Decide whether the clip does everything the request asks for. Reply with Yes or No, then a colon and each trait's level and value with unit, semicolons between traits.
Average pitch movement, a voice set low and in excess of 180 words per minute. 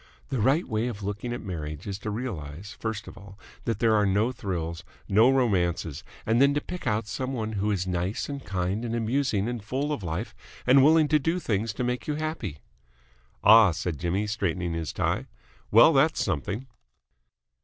Yes: average, 4.8 semitones; low, 105 Hz; average, 190 wpm